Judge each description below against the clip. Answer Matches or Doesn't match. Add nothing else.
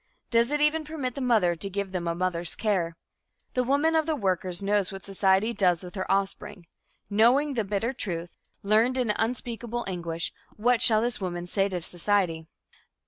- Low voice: Doesn't match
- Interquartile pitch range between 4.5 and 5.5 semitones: Matches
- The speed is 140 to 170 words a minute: Doesn't match